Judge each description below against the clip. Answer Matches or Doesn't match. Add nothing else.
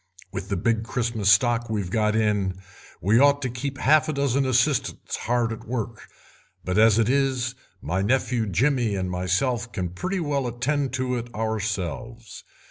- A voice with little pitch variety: Doesn't match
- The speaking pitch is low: Matches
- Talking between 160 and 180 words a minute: Matches